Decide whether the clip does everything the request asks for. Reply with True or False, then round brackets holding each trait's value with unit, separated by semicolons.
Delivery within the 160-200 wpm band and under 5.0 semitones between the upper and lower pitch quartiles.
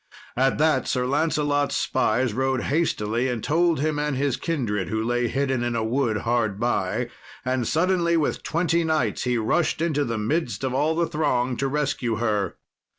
True (175 wpm; 4.5 semitones)